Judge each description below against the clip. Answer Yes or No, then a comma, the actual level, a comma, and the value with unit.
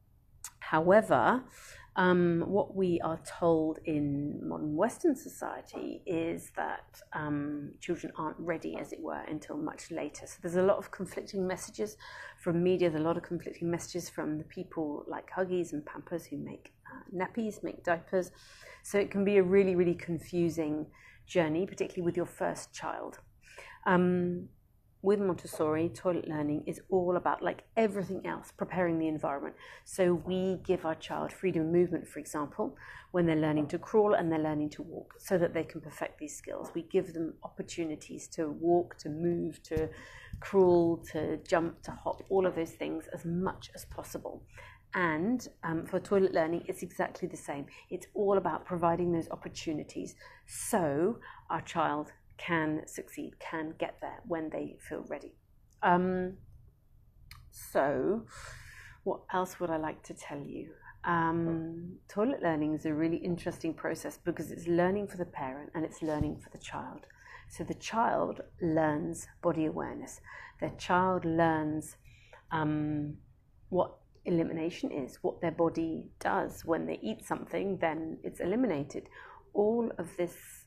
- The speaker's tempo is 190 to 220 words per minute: No, average, 155 wpm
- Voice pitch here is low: No, medium, 170 Hz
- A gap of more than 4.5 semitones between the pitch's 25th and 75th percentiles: No, narrow, 2.6 semitones